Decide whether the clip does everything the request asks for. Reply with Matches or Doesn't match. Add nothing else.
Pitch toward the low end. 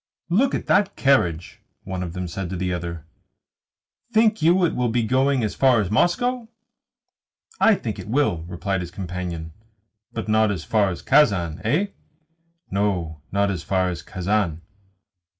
Matches